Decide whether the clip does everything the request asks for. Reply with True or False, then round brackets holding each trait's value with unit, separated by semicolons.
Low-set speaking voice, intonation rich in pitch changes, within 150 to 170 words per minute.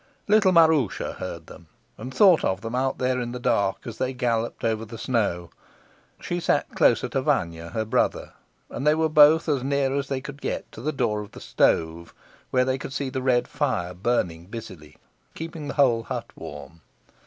False (125 Hz; 5.9 semitones; 195 wpm)